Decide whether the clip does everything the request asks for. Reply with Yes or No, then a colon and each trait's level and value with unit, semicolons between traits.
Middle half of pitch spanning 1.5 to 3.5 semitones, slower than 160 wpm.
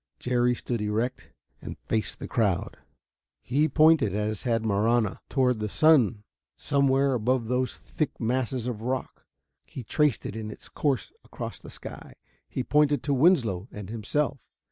No: average, 4.1 semitones; average, 150 wpm